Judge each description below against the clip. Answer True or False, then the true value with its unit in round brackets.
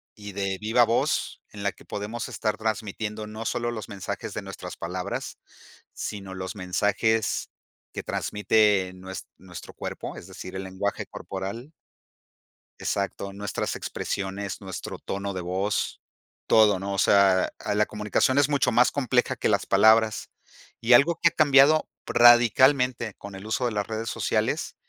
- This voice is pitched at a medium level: False (105 Hz)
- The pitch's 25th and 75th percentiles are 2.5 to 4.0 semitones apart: True (3.2 semitones)